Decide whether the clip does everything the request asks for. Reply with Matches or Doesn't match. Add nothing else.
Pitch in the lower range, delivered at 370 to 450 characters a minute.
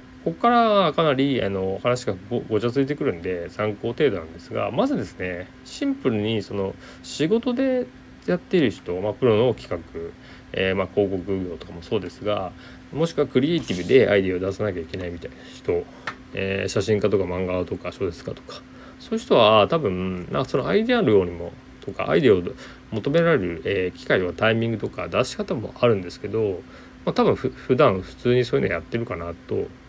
Matches